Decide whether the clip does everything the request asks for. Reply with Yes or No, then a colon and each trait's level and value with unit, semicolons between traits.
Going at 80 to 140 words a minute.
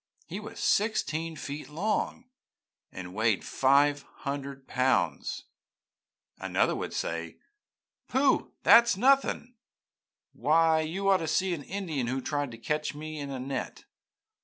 Yes: slow, 135 wpm